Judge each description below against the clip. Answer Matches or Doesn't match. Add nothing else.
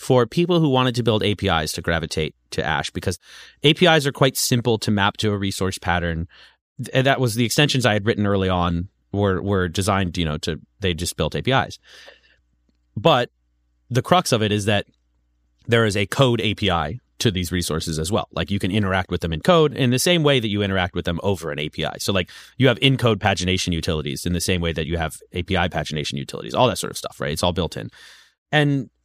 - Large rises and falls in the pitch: Matches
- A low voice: Matches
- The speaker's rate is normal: Doesn't match